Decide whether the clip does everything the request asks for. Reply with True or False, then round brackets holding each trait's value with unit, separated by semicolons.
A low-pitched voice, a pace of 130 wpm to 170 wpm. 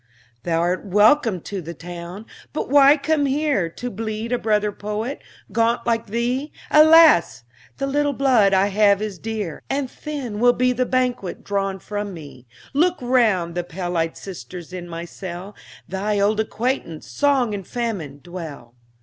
False (210 Hz; 160 wpm)